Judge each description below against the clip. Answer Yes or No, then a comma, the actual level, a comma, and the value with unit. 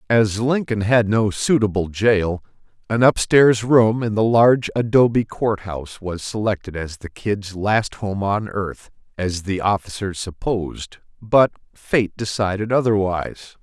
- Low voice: Yes, low, 105 Hz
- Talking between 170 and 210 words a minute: No, slow, 135 wpm